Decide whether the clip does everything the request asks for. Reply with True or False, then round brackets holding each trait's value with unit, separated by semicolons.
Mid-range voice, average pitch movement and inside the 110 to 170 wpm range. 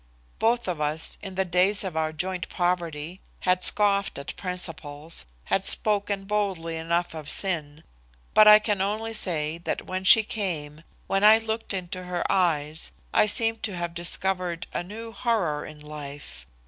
True (180 Hz; 4.1 semitones; 160 wpm)